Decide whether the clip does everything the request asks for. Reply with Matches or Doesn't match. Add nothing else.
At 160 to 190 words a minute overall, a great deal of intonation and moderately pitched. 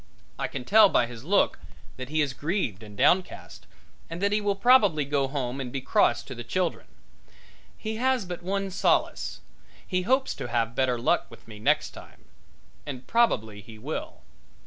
Matches